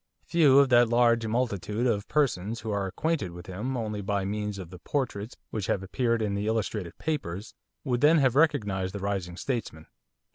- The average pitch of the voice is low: Yes, low, 110 Hz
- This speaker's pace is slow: No, average, 185 wpm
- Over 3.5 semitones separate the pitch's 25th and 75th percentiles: Yes, average, 4.3 semitones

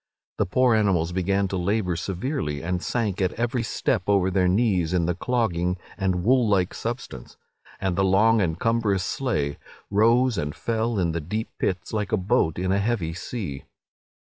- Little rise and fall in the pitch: No, average, 4.3 semitones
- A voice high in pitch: No, very low, 95 Hz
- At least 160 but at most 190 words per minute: Yes, average, 175 wpm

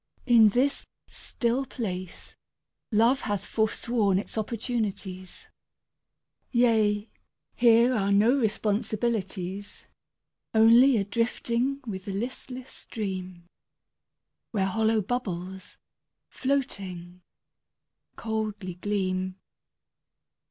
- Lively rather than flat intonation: No, average, 3.7 semitones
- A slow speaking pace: Yes, slow, 80 wpm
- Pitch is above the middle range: Yes, high, 215 Hz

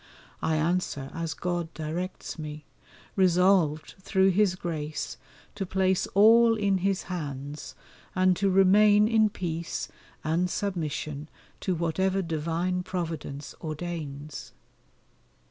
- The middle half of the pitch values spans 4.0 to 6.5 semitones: No, average, 3.5 semitones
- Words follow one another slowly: Yes, slow, 110 wpm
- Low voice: No, medium, 175 Hz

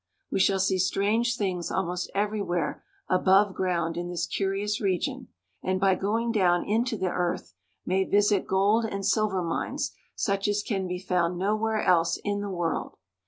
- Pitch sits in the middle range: No, high, 195 Hz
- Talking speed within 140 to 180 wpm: Yes, average, 165 wpm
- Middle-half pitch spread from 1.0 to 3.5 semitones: Yes, narrow, 2.4 semitones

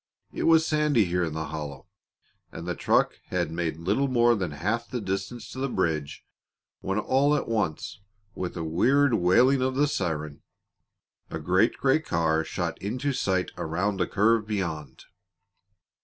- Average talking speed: Yes, average, 160 wpm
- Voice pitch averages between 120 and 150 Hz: No, very low, 95 Hz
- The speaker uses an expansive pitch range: Yes, wide, 7.2 semitones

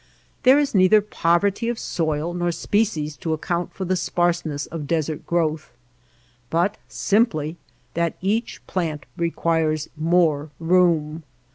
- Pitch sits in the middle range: Yes, medium, 170 Hz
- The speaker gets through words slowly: Yes, slow, 125 wpm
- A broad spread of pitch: No, average, 3.0 semitones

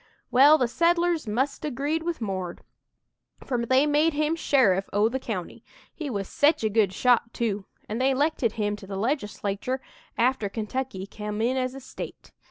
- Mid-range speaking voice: No, very high, 250 Hz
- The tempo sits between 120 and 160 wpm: No, average, 180 wpm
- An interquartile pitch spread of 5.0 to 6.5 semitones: Yes, wide, 5.4 semitones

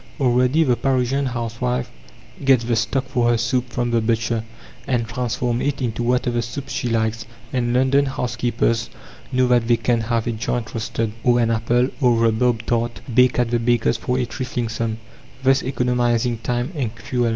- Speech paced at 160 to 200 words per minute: Yes, average, 175 wpm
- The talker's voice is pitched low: Yes, low, 120 Hz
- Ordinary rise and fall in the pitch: No, narrow, 1.5 semitones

